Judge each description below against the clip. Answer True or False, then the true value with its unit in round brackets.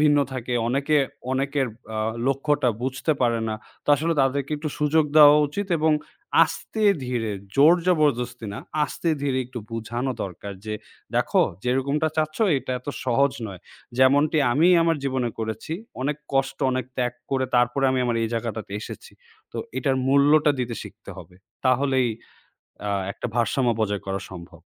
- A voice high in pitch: False (130 Hz)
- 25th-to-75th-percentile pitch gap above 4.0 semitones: False (3.4 semitones)